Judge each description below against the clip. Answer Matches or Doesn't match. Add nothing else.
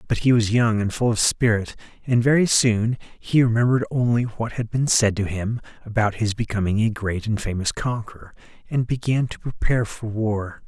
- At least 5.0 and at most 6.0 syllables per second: Matches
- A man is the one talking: Matches